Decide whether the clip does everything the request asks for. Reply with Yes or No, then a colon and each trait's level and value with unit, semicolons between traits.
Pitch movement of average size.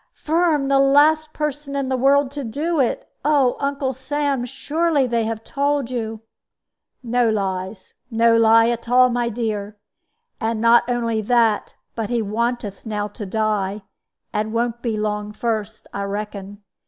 Yes: average, 4.1 semitones